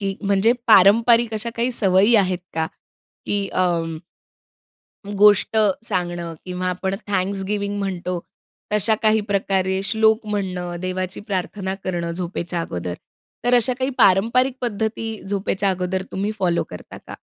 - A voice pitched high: Yes, high, 195 Hz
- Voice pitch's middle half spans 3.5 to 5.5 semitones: No, average, 2.9 semitones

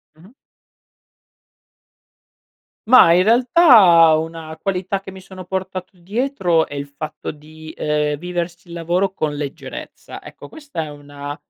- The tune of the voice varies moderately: Yes, average, 3.6 semitones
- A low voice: No, medium, 170 Hz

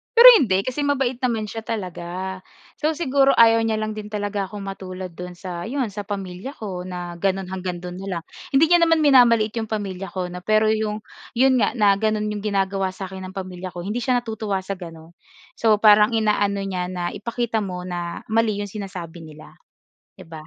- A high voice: Yes, high, 200 Hz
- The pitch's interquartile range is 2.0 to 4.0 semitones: Yes, average, 3.4 semitones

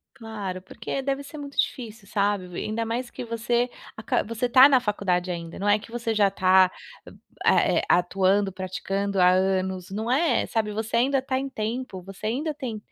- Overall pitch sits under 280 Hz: Yes, high, 215 Hz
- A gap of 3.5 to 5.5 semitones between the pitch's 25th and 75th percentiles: Yes, average, 4.2 semitones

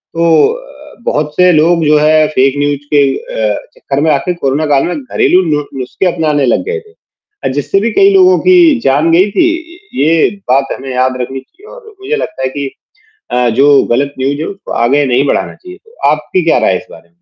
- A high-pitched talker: No, medium, 150 Hz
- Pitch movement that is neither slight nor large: No, wide, 7.2 semitones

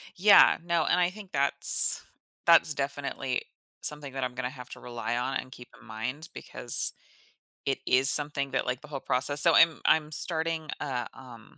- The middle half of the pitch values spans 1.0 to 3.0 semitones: No, average, 4.0 semitones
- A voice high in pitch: No, medium, 140 Hz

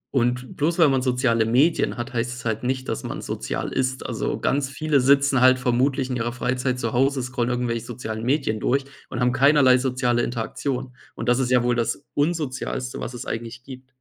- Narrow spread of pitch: Yes, narrow, 1.7 semitones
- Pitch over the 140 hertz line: No, low, 125 Hz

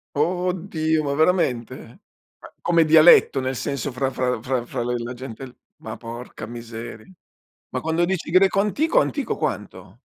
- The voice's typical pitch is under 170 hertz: Yes, medium, 140 Hz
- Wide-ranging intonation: Yes, wide, 6.0 semitones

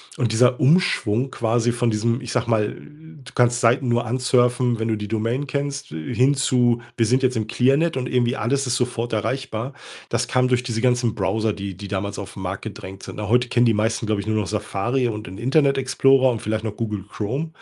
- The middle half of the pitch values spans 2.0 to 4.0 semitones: Yes, average, 2.8 semitones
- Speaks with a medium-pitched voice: No, low, 120 Hz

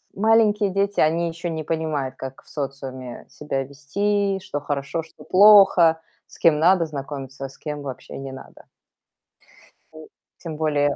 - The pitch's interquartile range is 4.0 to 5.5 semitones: Yes, average, 4.8 semitones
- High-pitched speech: No, medium, 155 Hz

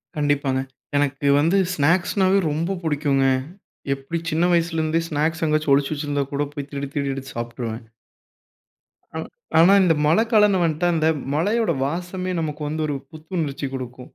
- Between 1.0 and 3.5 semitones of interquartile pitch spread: Yes, average, 3.1 semitones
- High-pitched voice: No, medium, 155 Hz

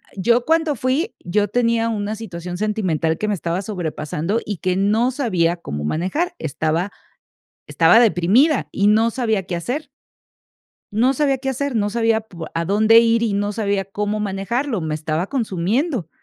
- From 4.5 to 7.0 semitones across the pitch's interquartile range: Yes, average, 4.8 semitones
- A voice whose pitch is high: Yes, high, 210 Hz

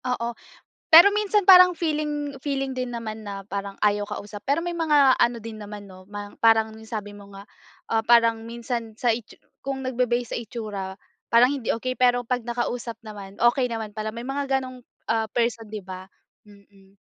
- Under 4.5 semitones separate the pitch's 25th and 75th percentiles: Yes, average, 3.6 semitones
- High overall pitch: Yes, high, 230 Hz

